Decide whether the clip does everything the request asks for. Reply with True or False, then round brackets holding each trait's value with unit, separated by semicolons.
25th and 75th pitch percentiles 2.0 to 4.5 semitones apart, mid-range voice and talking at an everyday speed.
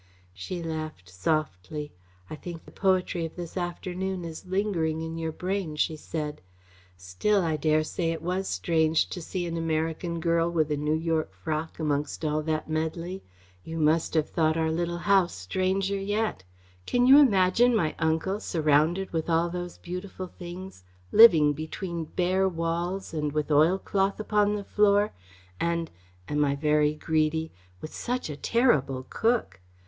True (3.2 semitones; 165 Hz; 160 wpm)